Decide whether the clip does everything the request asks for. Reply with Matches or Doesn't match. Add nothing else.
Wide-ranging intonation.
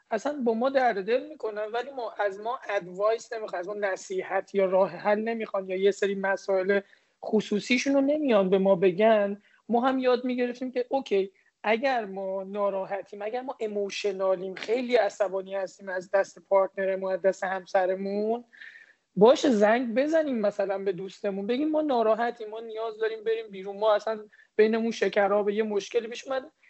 Doesn't match